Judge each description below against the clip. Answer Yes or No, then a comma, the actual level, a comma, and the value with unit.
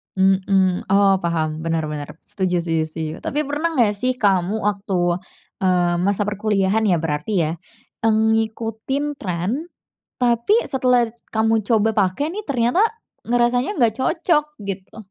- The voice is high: Yes, high, 205 Hz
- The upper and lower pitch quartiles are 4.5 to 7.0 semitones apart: Yes, average, 5.0 semitones